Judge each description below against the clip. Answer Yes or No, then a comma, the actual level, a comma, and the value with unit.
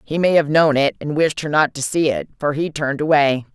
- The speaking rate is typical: No, fast, 270 wpm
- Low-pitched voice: No, medium, 150 Hz